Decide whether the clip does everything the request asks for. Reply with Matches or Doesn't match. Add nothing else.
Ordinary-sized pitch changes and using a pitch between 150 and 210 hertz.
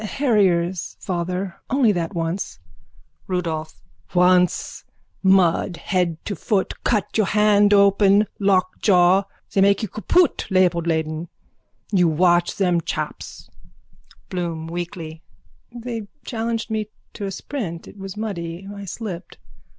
Matches